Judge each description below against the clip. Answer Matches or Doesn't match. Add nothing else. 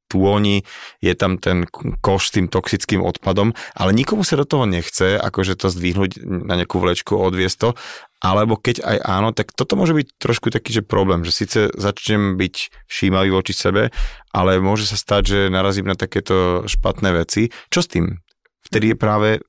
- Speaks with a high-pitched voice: Doesn't match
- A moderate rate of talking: Doesn't match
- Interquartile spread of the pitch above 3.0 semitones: Doesn't match